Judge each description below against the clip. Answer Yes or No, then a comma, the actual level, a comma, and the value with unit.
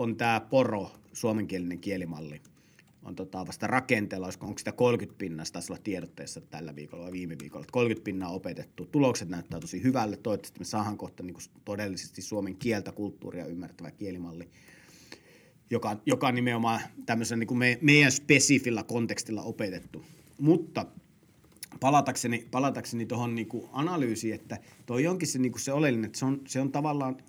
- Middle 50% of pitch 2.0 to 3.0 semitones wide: No, average, 5.1 semitones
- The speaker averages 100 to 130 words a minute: No, average, 145 wpm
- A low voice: Yes, low, 115 Hz